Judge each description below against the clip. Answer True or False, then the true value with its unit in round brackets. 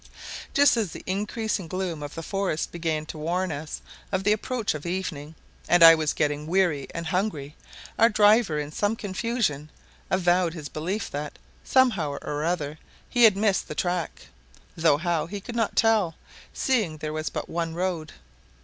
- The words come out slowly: False (170 wpm)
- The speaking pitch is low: False (175 Hz)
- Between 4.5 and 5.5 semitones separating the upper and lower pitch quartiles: True (4.8 semitones)